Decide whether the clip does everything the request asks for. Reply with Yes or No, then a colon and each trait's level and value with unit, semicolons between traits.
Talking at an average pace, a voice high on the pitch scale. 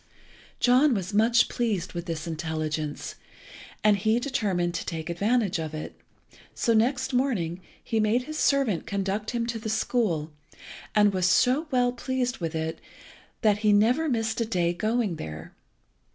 Yes: average, 155 wpm; high, 215 Hz